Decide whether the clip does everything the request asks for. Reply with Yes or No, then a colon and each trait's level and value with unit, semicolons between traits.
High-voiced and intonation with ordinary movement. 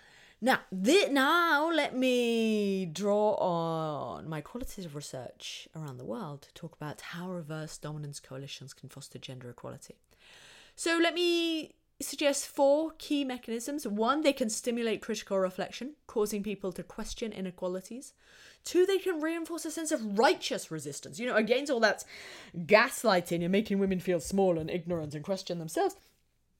No: high, 210 Hz; wide, 8.1 semitones